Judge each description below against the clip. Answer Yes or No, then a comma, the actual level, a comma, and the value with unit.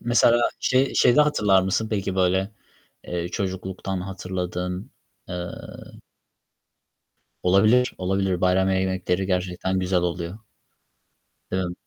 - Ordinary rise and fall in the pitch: No, narrow, 1.4 semitones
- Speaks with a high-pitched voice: No, very low, 95 Hz